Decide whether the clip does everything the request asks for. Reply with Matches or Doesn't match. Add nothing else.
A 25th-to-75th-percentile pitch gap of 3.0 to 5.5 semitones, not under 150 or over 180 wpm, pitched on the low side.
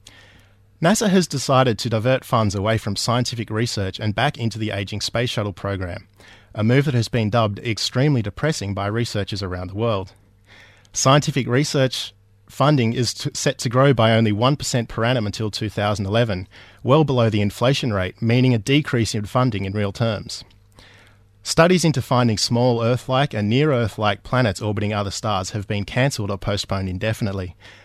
Matches